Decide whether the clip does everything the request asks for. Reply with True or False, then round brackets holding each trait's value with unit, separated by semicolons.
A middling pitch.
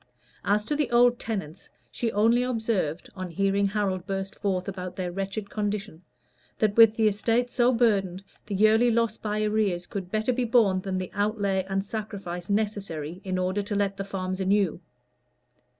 False (200 Hz)